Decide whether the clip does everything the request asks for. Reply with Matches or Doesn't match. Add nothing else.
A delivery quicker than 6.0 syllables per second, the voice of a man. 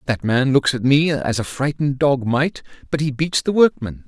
Doesn't match